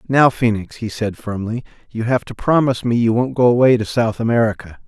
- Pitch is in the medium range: No, low, 115 Hz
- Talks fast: Yes, fast, 210 wpm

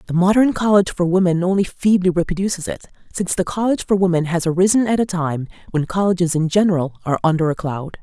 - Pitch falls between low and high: Yes, medium, 180 Hz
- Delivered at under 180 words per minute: No, average, 200 wpm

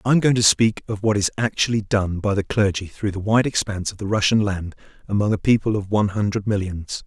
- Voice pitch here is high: No, low, 105 Hz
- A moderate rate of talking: No, fast, 240 wpm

